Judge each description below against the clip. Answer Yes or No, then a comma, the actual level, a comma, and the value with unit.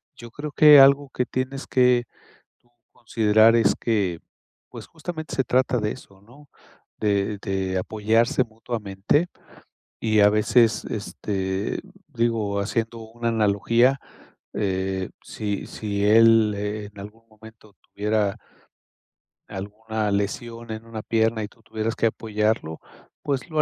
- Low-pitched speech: Yes, low, 110 Hz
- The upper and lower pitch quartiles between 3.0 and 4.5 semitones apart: No, narrow, 2.4 semitones